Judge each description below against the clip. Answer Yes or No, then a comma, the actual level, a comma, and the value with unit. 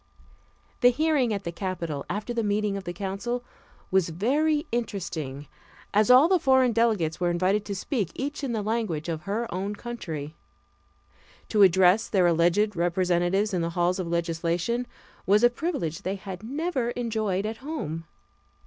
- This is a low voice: No, high, 200 Hz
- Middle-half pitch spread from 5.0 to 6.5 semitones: Yes, wide, 5.4 semitones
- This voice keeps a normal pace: Yes, average, 160 wpm